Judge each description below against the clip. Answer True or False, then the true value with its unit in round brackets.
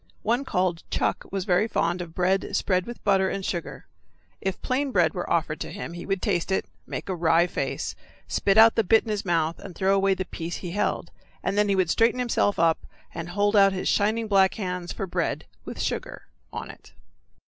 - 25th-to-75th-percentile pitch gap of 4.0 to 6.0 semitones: False (2.7 semitones)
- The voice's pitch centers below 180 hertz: False (190 Hz)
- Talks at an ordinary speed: False (215 wpm)